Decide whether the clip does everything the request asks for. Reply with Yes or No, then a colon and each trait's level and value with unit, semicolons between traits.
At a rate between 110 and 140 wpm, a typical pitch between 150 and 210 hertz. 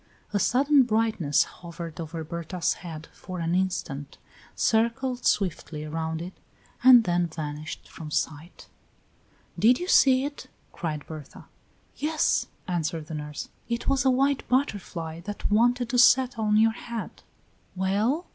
Yes: slow, 135 wpm; high, 190 Hz